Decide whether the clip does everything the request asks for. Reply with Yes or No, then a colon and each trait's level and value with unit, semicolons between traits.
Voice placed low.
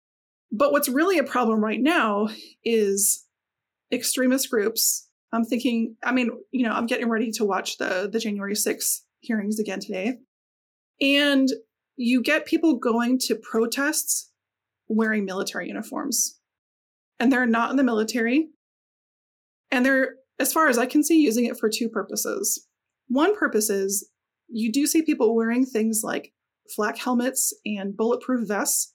No: high, 240 Hz